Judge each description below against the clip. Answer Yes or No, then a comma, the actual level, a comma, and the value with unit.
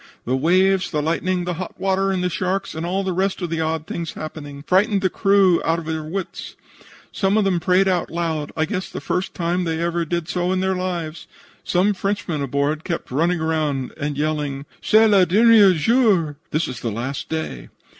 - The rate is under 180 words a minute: No, average, 200 wpm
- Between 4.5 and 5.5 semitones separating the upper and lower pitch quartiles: No, average, 3.3 semitones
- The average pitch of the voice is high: No, medium, 175 Hz